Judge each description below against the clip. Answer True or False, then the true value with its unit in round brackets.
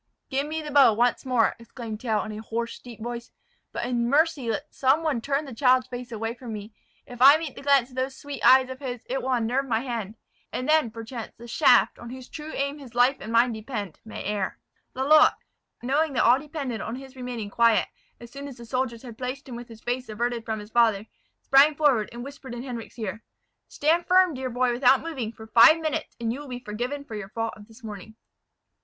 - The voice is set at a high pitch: True (245 Hz)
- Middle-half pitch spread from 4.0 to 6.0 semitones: False (3.1 semitones)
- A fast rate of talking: True (225 wpm)